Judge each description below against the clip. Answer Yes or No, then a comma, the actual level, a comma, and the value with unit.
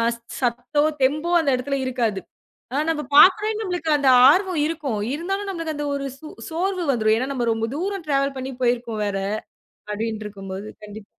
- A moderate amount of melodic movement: No, wide, 6.1 semitones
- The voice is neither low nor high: No, very high, 275 Hz